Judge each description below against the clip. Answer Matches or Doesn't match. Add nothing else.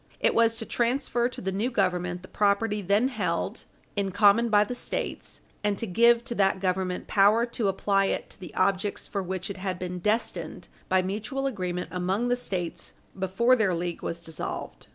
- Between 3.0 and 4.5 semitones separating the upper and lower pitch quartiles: Matches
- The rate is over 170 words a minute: Matches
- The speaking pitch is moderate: Doesn't match